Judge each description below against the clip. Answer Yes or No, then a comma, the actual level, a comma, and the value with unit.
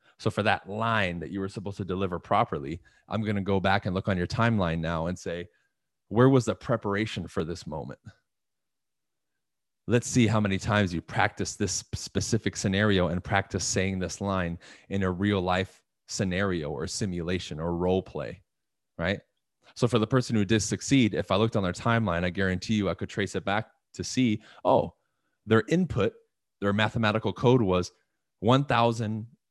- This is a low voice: Yes, low, 100 Hz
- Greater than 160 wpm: Yes, average, 180 wpm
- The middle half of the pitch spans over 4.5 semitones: No, average, 3.4 semitones